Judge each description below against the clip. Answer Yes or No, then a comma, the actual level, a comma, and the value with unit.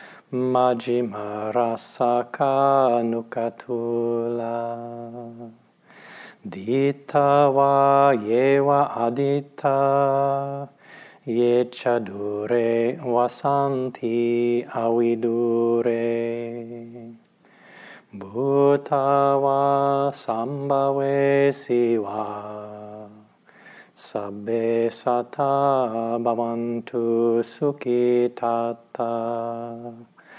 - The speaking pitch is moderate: No, low, 120 Hz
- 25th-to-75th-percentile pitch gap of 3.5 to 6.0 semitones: No, average, 2.9 semitones